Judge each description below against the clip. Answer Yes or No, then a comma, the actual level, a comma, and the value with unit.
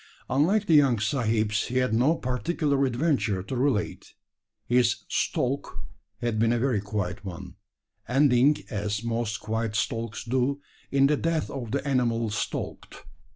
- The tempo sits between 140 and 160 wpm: Yes, average, 145 wpm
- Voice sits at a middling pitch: No, low, 120 Hz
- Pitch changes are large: No, average, 4.1 semitones